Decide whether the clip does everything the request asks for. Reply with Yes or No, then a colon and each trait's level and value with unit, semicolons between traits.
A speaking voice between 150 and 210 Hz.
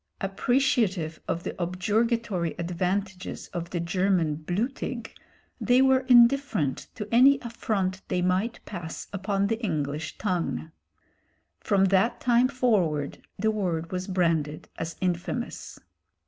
Yes: high, 190 Hz